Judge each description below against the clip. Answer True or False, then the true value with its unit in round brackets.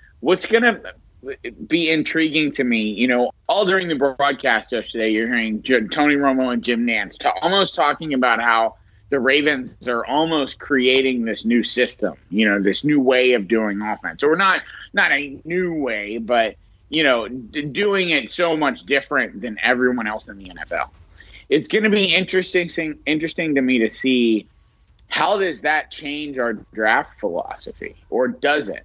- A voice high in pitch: False (135 Hz)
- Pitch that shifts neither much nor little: False (5.7 semitones)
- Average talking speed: True (170 wpm)